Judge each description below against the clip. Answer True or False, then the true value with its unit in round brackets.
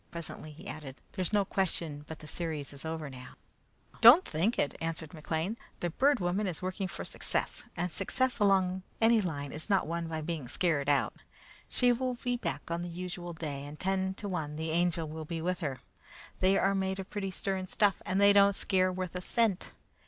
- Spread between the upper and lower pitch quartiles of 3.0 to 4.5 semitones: True (3.6 semitones)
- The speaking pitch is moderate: True (180 Hz)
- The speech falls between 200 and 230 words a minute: True (205 wpm)